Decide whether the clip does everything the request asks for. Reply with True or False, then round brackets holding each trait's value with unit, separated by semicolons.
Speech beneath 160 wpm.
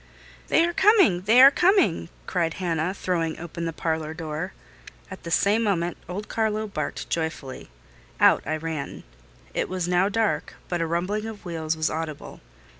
False (165 wpm)